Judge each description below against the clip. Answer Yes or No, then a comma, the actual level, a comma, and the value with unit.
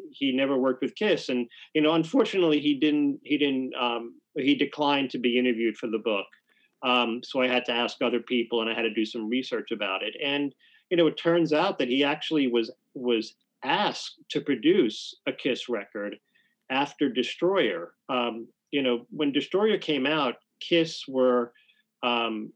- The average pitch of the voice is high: No, low, 135 Hz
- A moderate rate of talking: Yes, average, 180 wpm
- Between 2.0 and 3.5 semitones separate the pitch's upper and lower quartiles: No, average, 4.0 semitones